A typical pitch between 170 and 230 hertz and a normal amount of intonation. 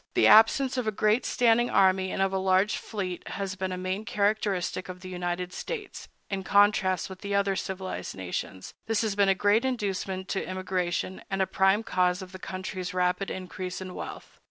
No: high, 190 Hz; narrow, 1.7 semitones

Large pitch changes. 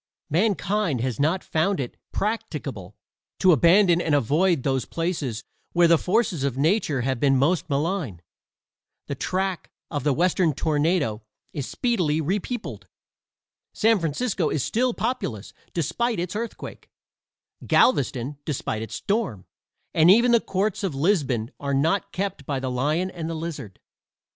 Yes: wide, 5.9 semitones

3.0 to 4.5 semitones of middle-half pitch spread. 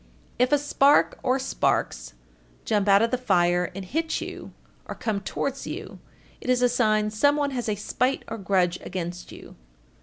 No: average, 5.3 semitones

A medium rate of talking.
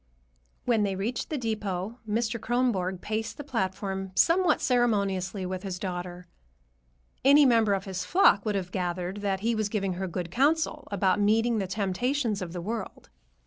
Yes: average, 165 wpm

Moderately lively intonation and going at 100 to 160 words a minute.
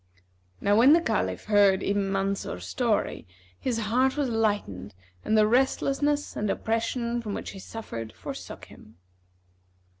Yes: average, 3.7 semitones; average, 140 wpm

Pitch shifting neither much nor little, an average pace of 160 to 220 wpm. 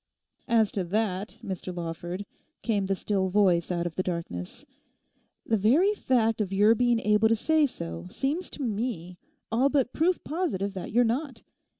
Yes: average, 5.0 semitones; average, 170 wpm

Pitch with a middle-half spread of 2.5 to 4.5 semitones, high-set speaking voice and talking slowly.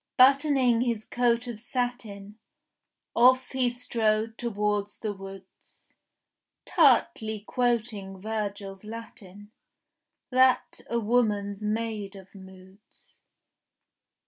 Yes: average, 3.2 semitones; high, 220 Hz; slow, 90 wpm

